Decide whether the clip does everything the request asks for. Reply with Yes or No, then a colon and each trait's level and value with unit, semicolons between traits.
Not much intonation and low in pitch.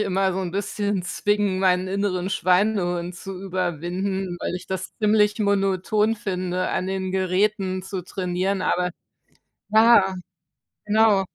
No: narrow, 1.9 semitones; high, 190 Hz